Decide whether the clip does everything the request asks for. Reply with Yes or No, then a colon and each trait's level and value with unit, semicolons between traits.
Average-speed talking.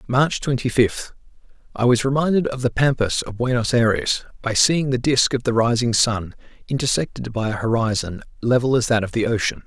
Yes: average, 180 wpm